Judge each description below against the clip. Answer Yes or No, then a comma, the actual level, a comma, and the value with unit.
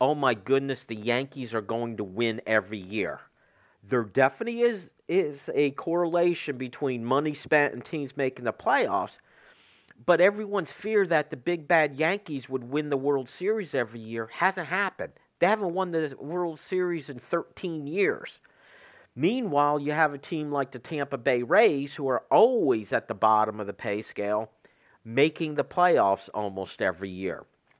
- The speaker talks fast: No, average, 165 wpm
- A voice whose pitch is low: No, medium, 145 Hz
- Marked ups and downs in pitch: Yes, wide, 6.5 semitones